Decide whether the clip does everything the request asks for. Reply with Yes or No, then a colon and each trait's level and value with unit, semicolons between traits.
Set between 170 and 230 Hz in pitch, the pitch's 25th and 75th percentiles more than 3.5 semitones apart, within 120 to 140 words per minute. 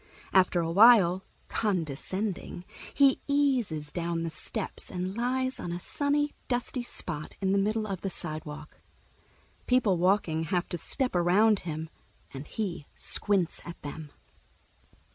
Yes: medium, 185 Hz; average, 5.1 semitones; slow, 135 wpm